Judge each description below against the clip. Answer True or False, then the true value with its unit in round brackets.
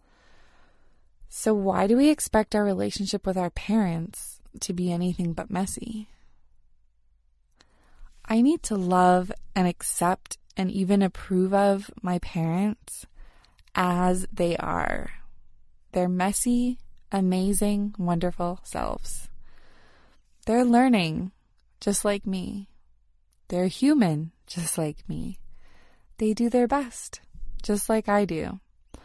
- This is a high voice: True (195 Hz)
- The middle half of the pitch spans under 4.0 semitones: True (3.3 semitones)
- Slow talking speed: True (110 wpm)